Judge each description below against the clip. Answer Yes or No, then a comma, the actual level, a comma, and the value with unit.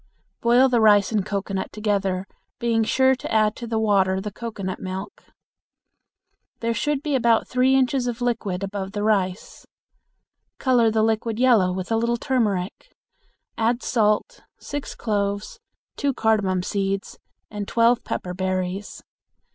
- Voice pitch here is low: No, high, 215 Hz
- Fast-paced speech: No, average, 140 wpm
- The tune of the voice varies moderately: Yes, average, 3.3 semitones